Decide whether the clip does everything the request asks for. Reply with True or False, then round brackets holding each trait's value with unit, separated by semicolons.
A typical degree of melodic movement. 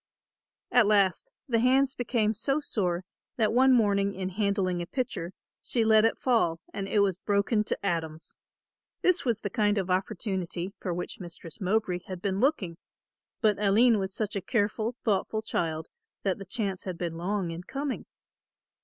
True (3.5 semitones)